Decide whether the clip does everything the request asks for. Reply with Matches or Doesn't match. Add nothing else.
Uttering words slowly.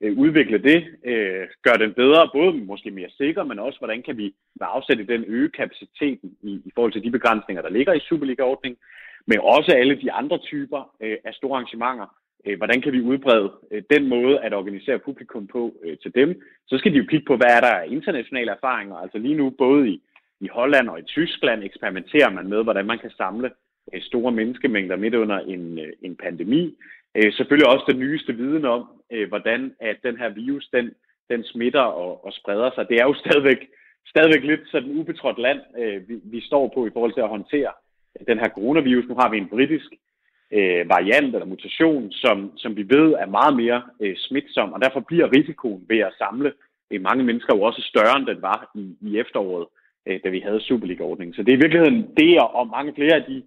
Doesn't match